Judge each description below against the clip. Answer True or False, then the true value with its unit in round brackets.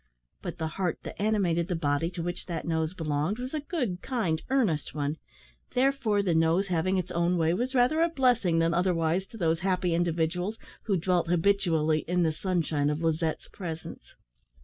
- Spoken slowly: False (180 wpm)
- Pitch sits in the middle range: True (175 Hz)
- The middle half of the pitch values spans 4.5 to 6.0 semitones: False (3.6 semitones)